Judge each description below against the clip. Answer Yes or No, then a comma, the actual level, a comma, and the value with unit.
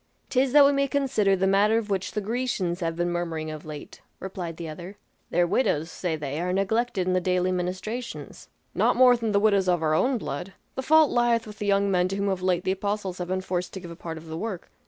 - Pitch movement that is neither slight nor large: Yes, average, 3.8 semitones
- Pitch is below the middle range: No, high, 190 Hz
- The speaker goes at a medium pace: No, fast, 245 wpm